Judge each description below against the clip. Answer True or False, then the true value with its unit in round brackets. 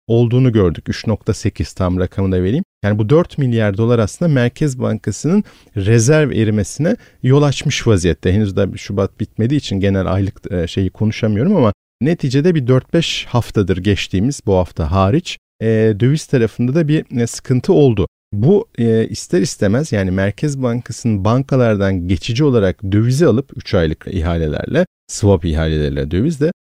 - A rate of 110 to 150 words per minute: True (135 wpm)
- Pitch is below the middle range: True (110 Hz)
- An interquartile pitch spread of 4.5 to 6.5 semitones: True (5.2 semitones)